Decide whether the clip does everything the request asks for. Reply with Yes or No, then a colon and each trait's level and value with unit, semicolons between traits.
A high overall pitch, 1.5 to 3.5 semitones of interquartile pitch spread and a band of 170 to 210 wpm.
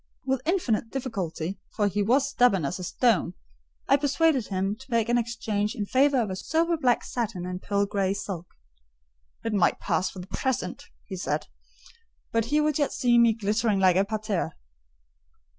No: high, 220 Hz; average, 4.8 semitones; average, 175 wpm